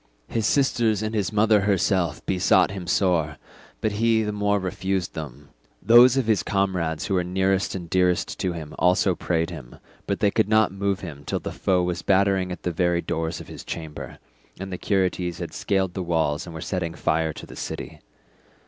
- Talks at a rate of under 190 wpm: No, average, 195 wpm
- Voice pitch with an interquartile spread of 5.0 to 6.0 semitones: No, average, 2.9 semitones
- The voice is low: Yes, very low, 95 Hz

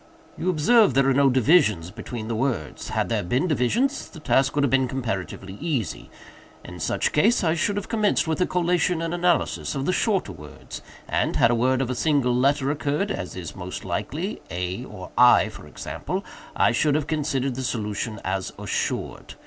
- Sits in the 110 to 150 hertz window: Yes, low, 135 Hz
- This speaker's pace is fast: No, average, 190 wpm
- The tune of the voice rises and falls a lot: Yes, wide, 6.2 semitones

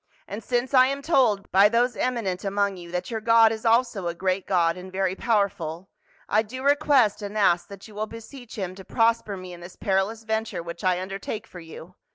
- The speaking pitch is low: No, high, 205 Hz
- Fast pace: Yes, fast, 215 wpm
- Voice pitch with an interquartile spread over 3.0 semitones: Yes, average, 3.6 semitones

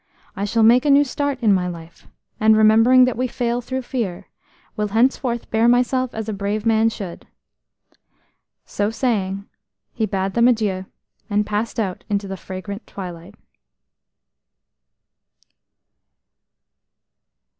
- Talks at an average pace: No, slow, 125 wpm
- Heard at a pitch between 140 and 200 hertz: No, high, 220 Hz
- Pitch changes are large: No, average, 3.4 semitones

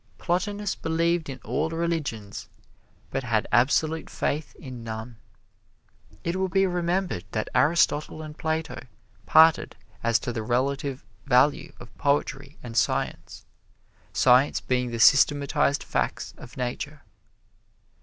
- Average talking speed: No, slow, 120 wpm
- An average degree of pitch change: Yes, average, 4.6 semitones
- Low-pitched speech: No, medium, 145 Hz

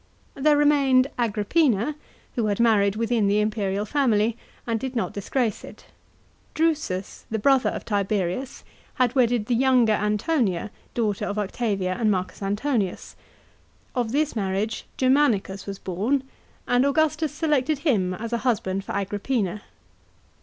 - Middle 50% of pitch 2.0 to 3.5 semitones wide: No, average, 4.8 semitones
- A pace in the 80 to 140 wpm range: Yes, slow, 135 wpm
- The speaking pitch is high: Yes, high, 225 Hz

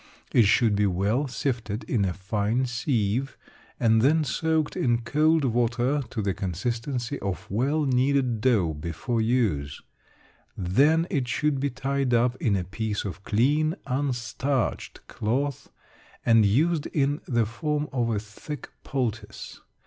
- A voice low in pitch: Yes, low, 120 Hz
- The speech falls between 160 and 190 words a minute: No, average, 140 wpm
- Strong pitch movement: No, average, 4.7 semitones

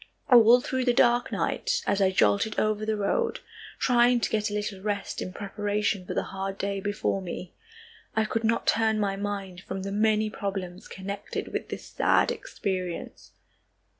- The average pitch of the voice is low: No, high, 205 Hz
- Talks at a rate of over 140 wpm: Yes, average, 170 wpm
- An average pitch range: No, narrow, 2.2 semitones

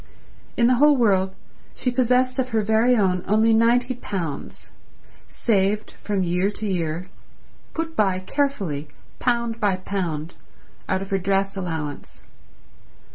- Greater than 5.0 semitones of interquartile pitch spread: No, average, 4.4 semitones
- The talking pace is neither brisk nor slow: No, slow, 130 wpm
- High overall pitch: Yes, high, 205 Hz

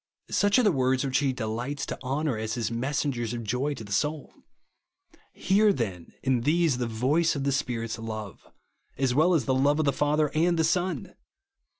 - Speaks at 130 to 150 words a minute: No, average, 195 wpm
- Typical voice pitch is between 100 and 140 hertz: Yes, low, 135 Hz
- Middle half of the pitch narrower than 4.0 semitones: No, average, 4.6 semitones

